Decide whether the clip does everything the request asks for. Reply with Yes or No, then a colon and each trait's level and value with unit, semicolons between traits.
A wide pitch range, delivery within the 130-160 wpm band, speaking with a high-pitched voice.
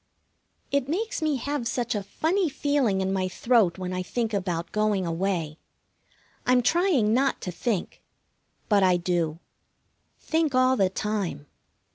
Yes: wide, 6.4 semitones; average, 145 wpm; high, 210 Hz